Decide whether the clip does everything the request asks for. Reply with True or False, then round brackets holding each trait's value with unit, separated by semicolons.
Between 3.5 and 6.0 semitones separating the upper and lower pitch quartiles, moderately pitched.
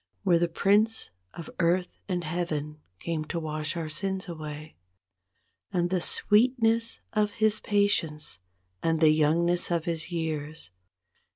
True (3.8 semitones; 170 Hz)